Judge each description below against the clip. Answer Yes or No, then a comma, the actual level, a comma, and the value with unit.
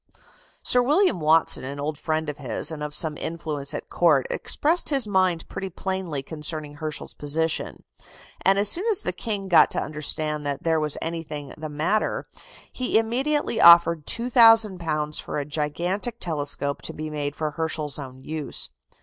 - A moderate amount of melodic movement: Yes, average, 4.4 semitones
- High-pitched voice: No, medium, 160 Hz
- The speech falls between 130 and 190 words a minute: Yes, average, 165 wpm